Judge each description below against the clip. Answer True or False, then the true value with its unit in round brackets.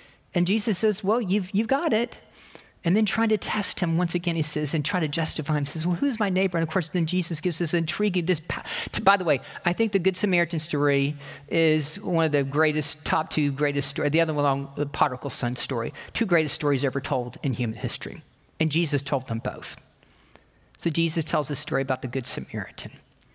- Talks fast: True (225 wpm)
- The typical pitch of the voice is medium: True (160 Hz)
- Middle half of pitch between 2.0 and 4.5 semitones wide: True (4.2 semitones)